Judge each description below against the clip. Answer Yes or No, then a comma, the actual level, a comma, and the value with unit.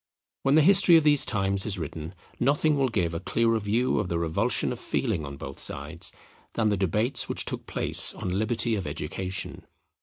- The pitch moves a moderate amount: No, wide, 6.4 semitones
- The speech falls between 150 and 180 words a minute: No, average, 190 wpm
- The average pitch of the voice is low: Yes, low, 105 Hz